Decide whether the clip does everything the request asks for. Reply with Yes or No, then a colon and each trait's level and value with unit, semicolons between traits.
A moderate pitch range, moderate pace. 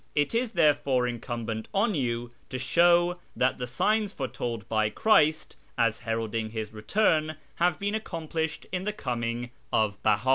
No: wide, 6.9 semitones; average, 150 wpm